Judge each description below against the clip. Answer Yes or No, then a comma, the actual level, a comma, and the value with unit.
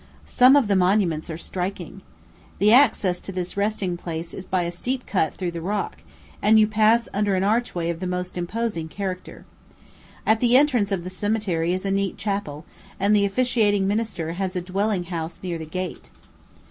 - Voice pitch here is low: No, high, 195 Hz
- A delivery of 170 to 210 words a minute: Yes, average, 185 wpm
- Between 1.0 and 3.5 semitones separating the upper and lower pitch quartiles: Yes, average, 3.2 semitones